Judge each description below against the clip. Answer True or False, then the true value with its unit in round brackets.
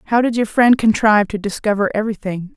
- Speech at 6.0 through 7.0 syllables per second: True (6.4 syllables/s)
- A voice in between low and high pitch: False (215 Hz)